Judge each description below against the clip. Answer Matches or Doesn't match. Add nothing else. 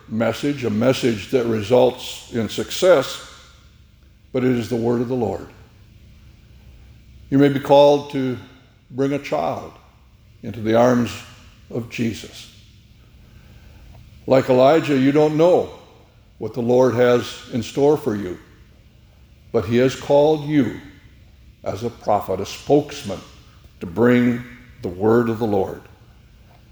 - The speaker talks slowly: Matches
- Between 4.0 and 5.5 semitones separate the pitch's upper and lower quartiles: Doesn't match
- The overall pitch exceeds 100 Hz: Matches